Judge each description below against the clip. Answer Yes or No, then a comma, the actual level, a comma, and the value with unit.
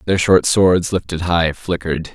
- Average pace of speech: Yes, average, 170 wpm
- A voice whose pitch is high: No, very low, 85 Hz